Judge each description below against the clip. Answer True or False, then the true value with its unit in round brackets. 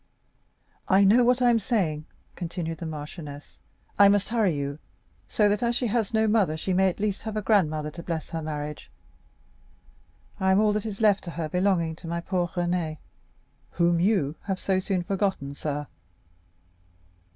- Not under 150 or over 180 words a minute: True (175 wpm)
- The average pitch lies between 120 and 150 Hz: False (185 Hz)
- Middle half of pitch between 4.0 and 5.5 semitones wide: True (4.5 semitones)